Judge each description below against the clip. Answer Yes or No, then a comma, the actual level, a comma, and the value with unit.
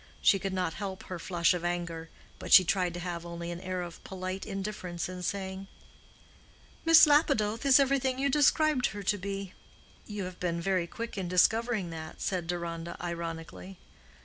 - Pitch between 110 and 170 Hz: No, medium, 185 Hz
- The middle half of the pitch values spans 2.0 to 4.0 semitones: Yes, average, 3.3 semitones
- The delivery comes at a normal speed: Yes, average, 175 wpm